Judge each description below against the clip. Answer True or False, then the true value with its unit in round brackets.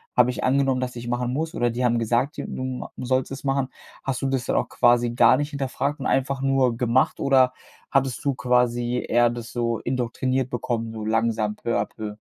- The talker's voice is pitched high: False (125 Hz)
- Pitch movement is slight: True (1.9 semitones)